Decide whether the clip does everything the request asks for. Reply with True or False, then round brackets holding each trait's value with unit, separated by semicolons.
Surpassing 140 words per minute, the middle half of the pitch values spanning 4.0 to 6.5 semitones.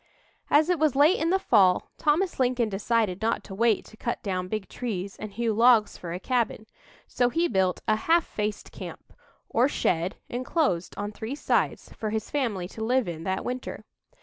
True (190 wpm; 4.6 semitones)